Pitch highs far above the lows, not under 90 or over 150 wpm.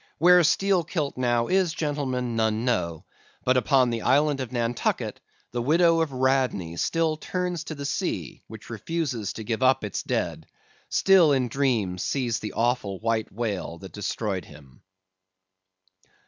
Yes: wide, 5.7 semitones; average, 145 wpm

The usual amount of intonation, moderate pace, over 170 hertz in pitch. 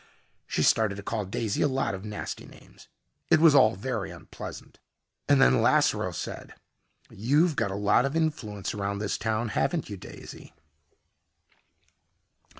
No: average, 5.0 semitones; average, 150 wpm; low, 110 Hz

